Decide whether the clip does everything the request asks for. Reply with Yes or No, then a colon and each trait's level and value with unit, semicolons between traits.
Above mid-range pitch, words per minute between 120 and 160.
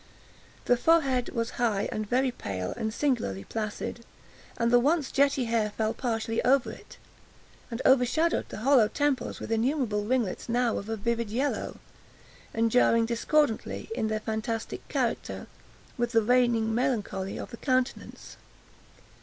Yes: high, 235 Hz; average, 145 wpm